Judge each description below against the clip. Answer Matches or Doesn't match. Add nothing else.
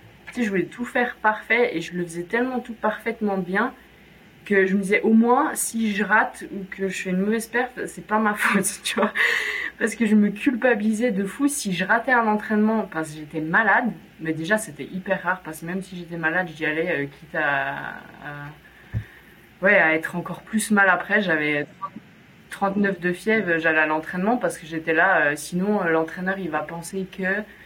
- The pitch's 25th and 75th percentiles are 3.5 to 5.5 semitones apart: Matches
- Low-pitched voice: Doesn't match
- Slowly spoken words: Doesn't match